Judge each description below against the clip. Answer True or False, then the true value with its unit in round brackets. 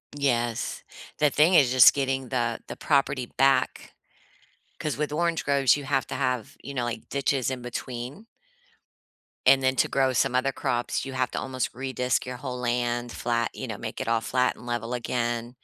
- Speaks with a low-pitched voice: True (130 Hz)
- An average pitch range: False (2.1 semitones)